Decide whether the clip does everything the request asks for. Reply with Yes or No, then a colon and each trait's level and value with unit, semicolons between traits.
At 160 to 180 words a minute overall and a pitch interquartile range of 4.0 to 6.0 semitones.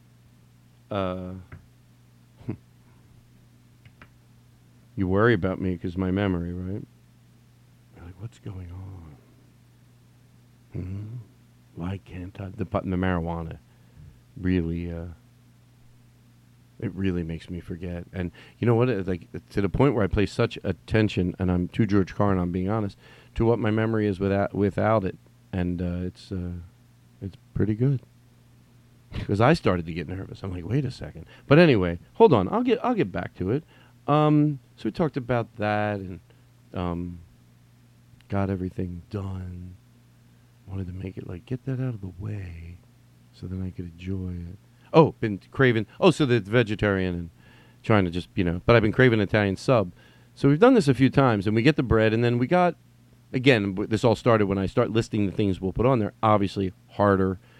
Yes: average, 175 wpm; average, 4.7 semitones